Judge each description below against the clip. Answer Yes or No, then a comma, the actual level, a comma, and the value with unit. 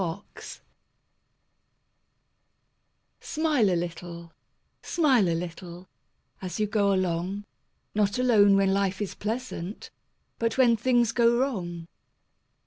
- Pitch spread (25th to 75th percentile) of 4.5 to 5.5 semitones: Yes, average, 4.8 semitones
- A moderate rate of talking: No, slow, 105 wpm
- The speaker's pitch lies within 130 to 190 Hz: No, high, 200 Hz